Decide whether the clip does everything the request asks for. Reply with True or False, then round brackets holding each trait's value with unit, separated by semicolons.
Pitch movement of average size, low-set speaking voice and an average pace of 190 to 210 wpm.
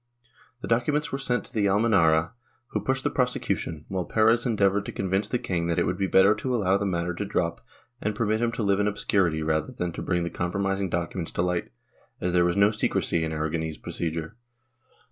True (4.1 semitones; 95 Hz; 205 wpm)